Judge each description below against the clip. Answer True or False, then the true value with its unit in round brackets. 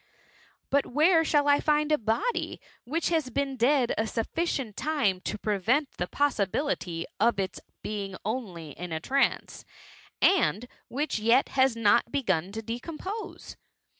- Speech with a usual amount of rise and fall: False (5.9 semitones)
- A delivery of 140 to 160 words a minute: True (150 wpm)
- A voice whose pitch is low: False (245 Hz)